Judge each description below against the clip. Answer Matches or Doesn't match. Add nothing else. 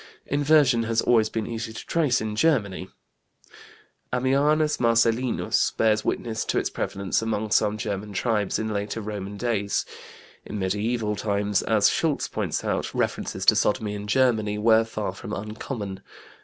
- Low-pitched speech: Matches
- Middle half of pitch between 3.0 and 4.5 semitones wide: Doesn't match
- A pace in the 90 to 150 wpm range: Matches